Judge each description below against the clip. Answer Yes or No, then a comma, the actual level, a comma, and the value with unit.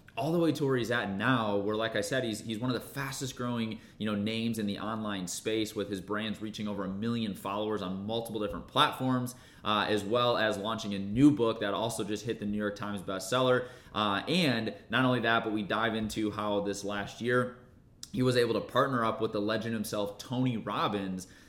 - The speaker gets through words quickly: Yes, fast, 225 wpm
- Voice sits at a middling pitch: No, low, 110 Hz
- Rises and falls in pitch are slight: No, average, 3.1 semitones